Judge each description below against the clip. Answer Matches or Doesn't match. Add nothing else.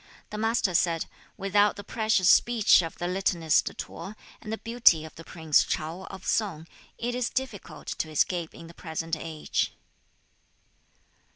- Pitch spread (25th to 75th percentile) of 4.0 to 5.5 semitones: Matches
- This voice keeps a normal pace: Matches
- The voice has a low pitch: Doesn't match